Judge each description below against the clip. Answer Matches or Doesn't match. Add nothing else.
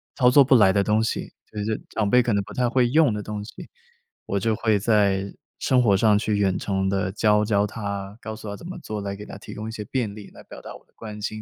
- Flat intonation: Matches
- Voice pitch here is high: Doesn't match